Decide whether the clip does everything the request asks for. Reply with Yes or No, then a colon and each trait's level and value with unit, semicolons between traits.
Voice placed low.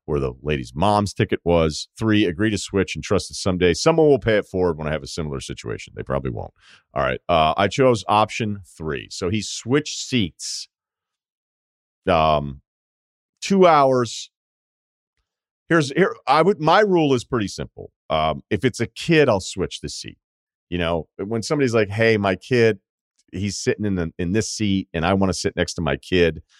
Yes: low, 100 Hz